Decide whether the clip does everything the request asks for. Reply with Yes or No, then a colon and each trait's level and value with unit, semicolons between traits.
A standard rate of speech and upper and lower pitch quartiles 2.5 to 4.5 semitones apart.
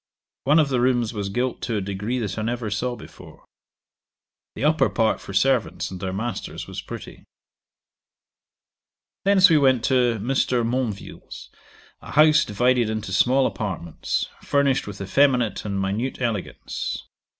Yes: average, 145 wpm; average, 4.1 semitones